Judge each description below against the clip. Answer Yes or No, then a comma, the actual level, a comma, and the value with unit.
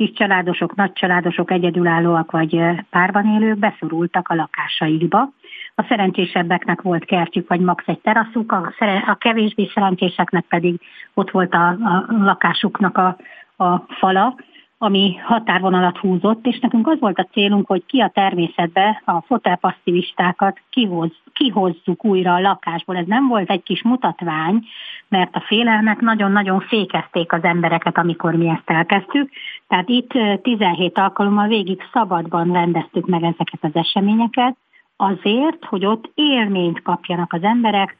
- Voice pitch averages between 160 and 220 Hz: Yes, high, 190 Hz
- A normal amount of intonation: Yes, average, 3.6 semitones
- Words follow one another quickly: No, average, 135 wpm